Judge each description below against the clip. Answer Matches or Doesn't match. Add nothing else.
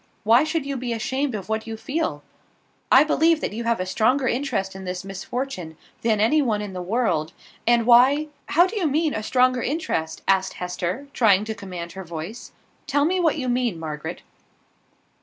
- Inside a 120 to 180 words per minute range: Doesn't match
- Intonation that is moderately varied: Doesn't match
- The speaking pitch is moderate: Doesn't match